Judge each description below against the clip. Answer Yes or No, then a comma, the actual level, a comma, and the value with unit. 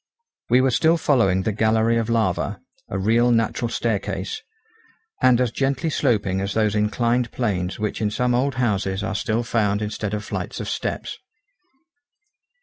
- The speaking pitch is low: Yes, low, 110 Hz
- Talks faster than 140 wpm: Yes, average, 155 wpm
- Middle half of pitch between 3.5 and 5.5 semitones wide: No, average, 2.8 semitones